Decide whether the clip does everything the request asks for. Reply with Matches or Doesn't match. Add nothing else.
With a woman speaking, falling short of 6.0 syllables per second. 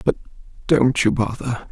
Doesn't match